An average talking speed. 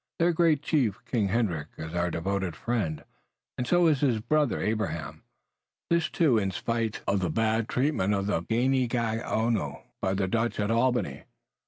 Yes: average, 160 wpm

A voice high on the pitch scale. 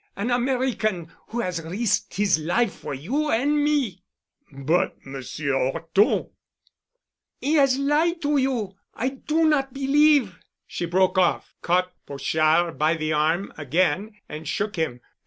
Yes: high, 195 Hz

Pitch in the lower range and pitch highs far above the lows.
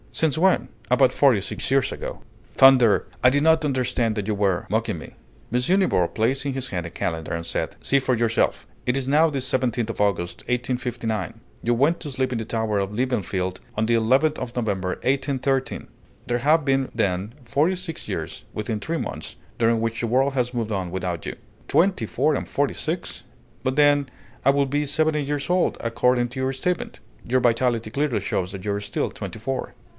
No: low, 125 Hz; average, 4.2 semitones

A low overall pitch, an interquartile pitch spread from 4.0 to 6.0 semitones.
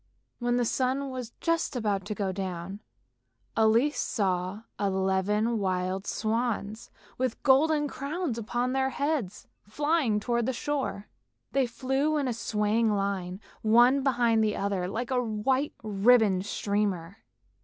No: high, 225 Hz; average, 4.5 semitones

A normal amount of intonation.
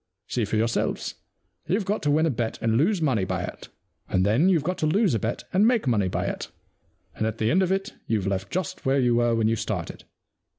No: wide, 8.4 semitones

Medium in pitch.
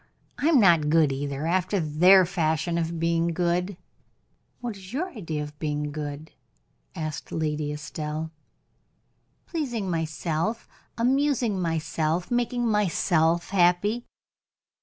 Yes: medium, 170 Hz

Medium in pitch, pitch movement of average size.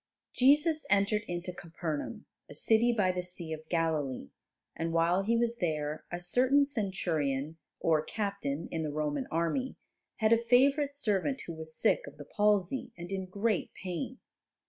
No: medium, 180 Hz; wide, 6.2 semitones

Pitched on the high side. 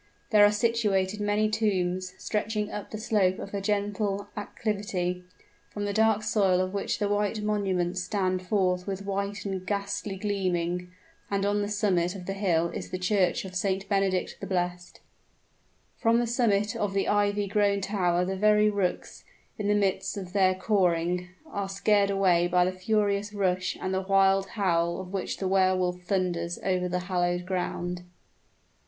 Yes: high, 195 Hz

